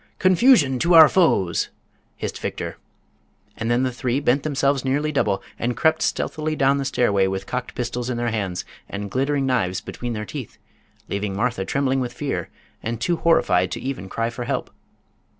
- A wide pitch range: No, average, 4.4 semitones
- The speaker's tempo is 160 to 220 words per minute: Yes, average, 175 wpm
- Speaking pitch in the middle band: No, low, 125 Hz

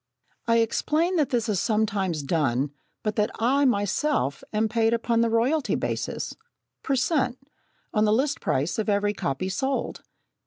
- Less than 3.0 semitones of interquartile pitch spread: No, average, 4.3 semitones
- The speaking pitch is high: Yes, high, 225 Hz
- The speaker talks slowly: No, average, 155 wpm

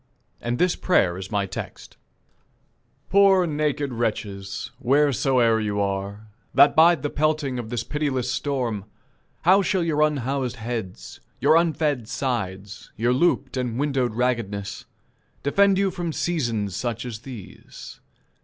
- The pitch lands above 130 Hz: No, low, 125 Hz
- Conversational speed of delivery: No, slow, 130 wpm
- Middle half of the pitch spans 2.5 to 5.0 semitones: No, wide, 5.5 semitones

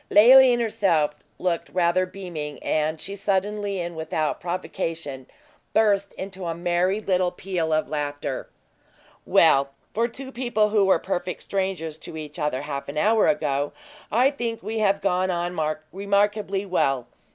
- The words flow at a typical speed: Yes, average, 145 wpm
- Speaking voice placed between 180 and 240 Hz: Yes, medium, 185 Hz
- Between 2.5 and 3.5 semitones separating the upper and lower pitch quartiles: No, average, 4.5 semitones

